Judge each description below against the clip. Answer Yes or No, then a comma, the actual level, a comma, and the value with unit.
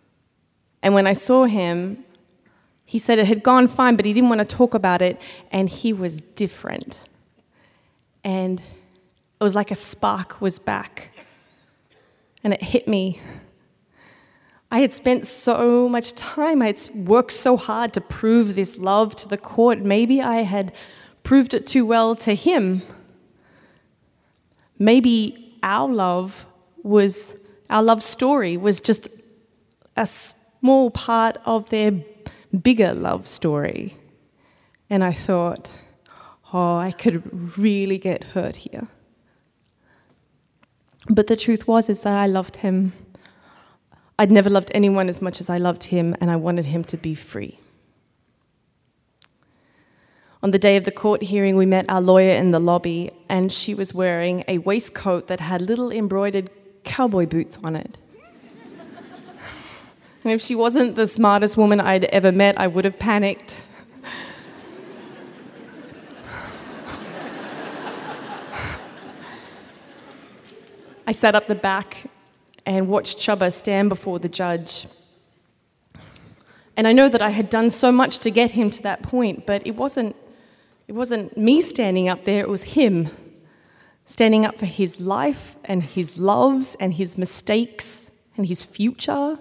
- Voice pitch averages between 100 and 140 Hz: No, high, 205 Hz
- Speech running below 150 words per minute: Yes, average, 140 wpm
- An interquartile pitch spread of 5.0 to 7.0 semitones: No, average, 3.5 semitones